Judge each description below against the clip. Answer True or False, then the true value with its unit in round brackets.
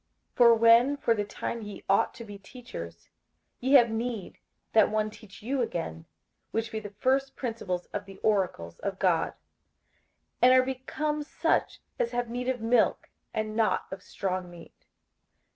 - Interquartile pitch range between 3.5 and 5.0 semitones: True (3.9 semitones)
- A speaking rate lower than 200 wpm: True (165 wpm)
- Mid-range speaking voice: False (225 Hz)